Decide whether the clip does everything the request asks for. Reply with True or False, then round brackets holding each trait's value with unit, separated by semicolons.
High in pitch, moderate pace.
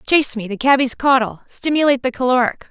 True (255 Hz; 180 wpm)